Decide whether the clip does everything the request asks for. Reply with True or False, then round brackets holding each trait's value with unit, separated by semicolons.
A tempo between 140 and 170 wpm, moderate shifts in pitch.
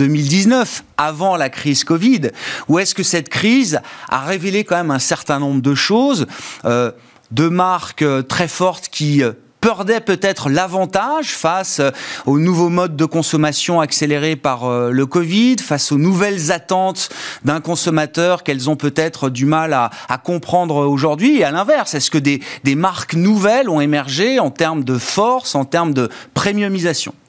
True (160 wpm; 4.7 semitones)